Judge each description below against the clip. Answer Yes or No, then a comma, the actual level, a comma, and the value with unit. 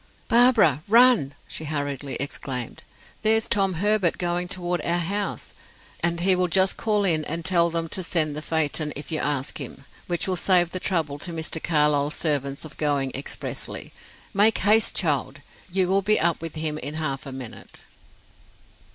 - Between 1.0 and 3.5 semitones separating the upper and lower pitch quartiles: No, average, 4.4 semitones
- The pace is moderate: Yes, average, 170 wpm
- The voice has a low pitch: No, medium, 165 Hz